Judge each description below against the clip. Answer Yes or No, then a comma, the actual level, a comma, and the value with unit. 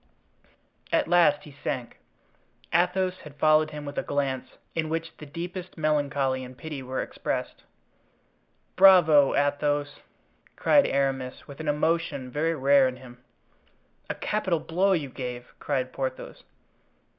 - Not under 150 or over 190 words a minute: No, slow, 135 wpm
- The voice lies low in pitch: No, medium, 145 Hz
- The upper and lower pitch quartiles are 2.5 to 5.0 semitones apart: Yes, average, 3.5 semitones